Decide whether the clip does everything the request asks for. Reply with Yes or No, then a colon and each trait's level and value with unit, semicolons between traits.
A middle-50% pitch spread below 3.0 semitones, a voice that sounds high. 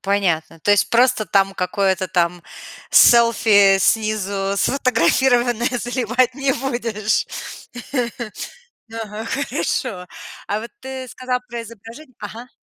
No: average, 3.8 semitones; high, 225 Hz